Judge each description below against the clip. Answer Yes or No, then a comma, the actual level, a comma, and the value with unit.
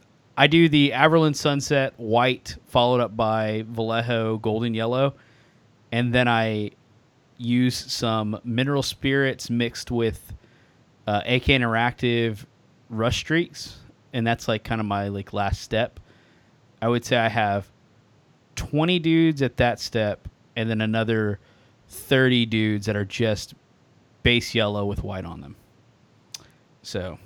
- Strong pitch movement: No, average, 2.9 semitones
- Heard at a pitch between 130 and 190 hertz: No, low, 115 Hz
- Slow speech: Yes, slow, 130 wpm